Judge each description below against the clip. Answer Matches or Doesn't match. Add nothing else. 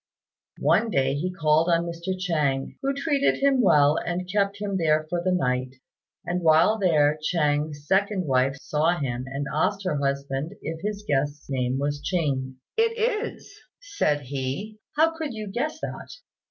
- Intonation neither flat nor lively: Doesn't match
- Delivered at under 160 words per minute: Doesn't match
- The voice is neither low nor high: Matches